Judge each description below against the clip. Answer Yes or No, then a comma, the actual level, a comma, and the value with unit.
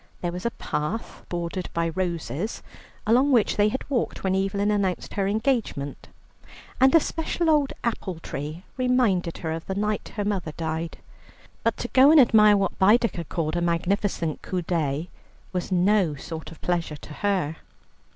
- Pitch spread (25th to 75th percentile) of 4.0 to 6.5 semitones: Yes, average, 4.4 semitones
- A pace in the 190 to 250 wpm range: No, average, 165 wpm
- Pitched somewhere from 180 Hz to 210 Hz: Yes, high, 190 Hz